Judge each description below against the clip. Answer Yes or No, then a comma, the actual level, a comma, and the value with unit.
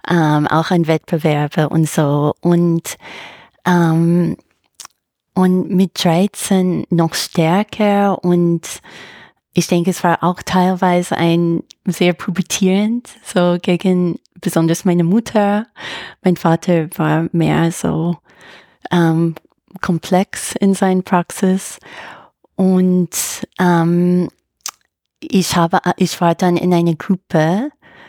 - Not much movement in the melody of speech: Yes, narrow, 2.0 semitones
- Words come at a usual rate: No, slow, 105 wpm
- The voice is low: No, medium, 175 Hz